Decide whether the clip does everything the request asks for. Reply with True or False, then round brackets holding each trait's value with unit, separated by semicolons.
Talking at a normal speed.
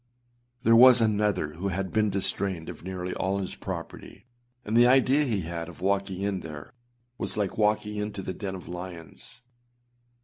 True (170 wpm)